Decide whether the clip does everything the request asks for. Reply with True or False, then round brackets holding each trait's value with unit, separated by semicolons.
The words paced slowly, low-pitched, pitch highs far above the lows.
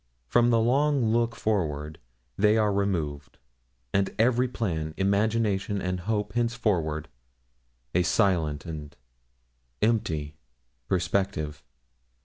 True (100 wpm; 100 Hz; 6.2 semitones)